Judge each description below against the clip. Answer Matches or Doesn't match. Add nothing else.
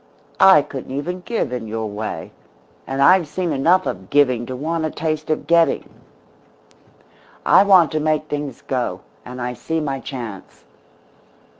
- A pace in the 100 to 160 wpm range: Matches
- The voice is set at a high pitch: Doesn't match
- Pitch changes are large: Doesn't match